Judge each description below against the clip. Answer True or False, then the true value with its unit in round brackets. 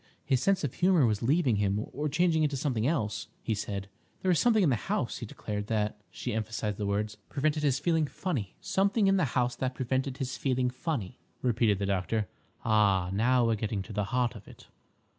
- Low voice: True (125 Hz)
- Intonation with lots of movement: True (5.8 semitones)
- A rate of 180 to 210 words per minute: True (200 wpm)